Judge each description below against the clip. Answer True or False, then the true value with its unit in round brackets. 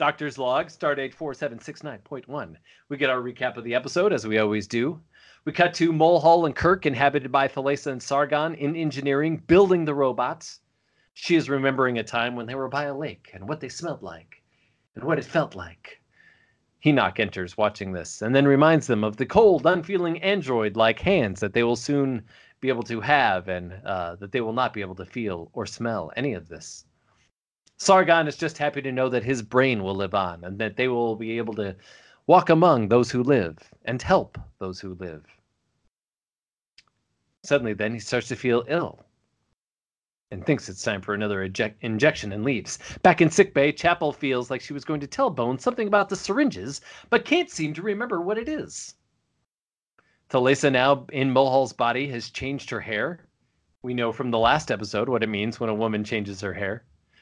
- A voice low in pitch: True (130 Hz)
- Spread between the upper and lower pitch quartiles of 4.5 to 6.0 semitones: True (5.0 semitones)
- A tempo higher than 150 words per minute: True (195 wpm)